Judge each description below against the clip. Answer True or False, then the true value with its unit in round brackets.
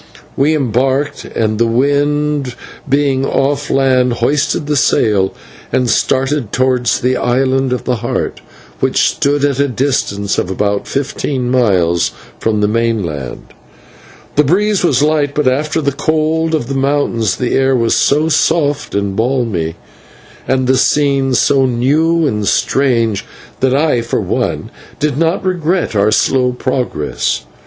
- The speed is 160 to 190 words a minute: False (145 wpm)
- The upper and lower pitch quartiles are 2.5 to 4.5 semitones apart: True (3.7 semitones)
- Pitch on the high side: False (130 Hz)